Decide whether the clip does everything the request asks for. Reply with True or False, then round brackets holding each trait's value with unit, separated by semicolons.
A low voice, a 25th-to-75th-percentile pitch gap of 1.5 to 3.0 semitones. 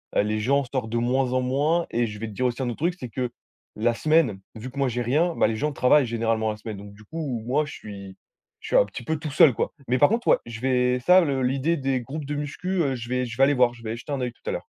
False (125 Hz; 3.7 semitones)